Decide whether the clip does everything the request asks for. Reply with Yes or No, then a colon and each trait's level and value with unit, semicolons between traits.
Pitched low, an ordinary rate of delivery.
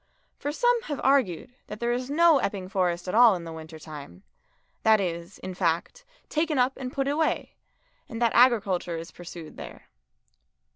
No: high, 215 Hz; average, 180 wpm